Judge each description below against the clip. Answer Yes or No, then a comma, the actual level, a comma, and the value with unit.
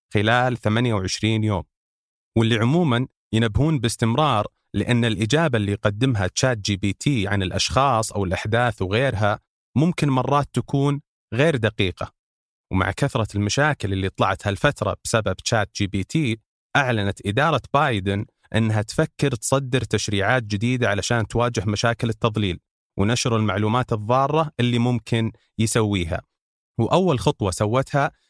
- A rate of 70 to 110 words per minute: No, average, 120 wpm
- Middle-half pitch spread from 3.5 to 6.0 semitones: Yes, average, 4.2 semitones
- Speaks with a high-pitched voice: No, low, 115 Hz